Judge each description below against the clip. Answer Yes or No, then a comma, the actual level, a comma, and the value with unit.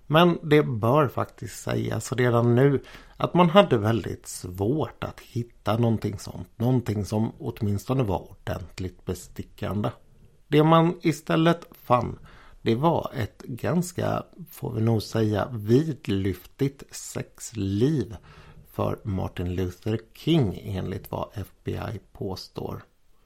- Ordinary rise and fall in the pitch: No, wide, 5.8 semitones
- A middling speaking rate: No, slow, 115 wpm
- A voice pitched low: Yes, low, 115 Hz